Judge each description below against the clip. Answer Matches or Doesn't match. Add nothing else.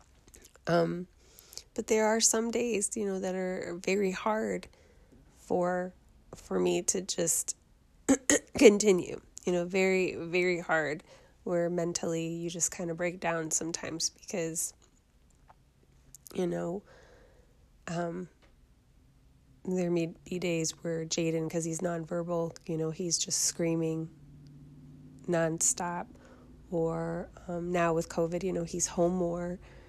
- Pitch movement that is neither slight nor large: Doesn't match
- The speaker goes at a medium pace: Doesn't match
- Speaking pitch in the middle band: Matches